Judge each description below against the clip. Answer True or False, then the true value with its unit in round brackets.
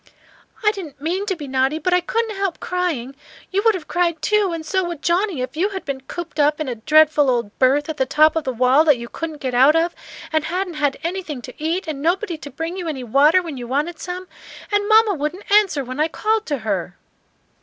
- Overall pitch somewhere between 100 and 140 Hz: False (315 Hz)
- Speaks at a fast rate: True (235 wpm)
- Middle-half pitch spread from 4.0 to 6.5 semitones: True (4.8 semitones)